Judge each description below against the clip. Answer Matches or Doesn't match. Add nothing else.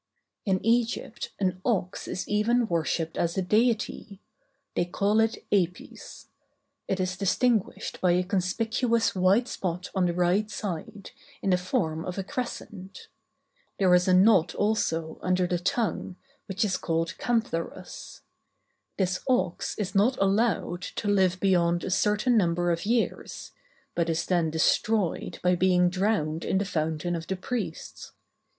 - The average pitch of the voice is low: Doesn't match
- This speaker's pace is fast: Doesn't match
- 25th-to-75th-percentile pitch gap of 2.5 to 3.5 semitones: Matches